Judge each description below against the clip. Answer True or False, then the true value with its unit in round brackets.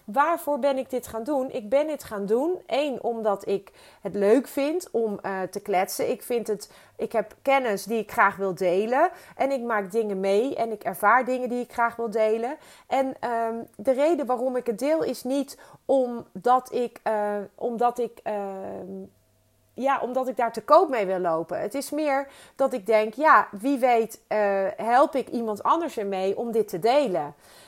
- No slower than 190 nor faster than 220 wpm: True (195 wpm)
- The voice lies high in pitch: True (235 Hz)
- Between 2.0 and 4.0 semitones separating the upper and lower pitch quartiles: False (4.6 semitones)